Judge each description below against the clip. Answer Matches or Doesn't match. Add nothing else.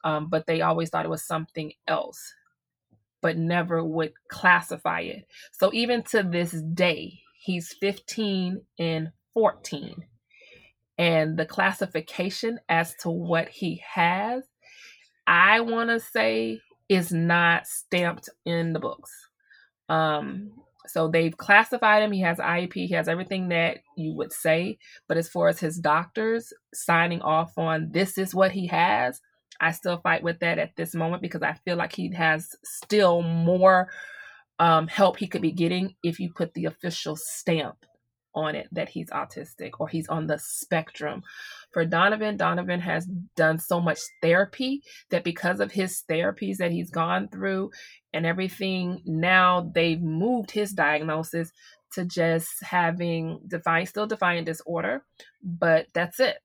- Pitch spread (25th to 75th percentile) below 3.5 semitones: Matches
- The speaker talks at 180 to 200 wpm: Doesn't match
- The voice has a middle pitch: Matches